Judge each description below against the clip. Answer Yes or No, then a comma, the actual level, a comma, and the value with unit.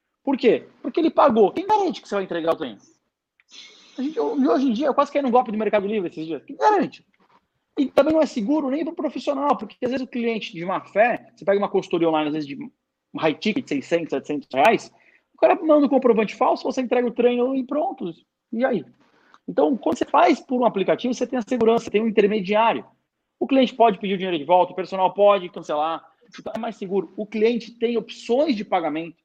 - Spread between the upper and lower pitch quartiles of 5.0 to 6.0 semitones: Yes, wide, 5.5 semitones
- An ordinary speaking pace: No, fast, 230 wpm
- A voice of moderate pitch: No, high, 230 Hz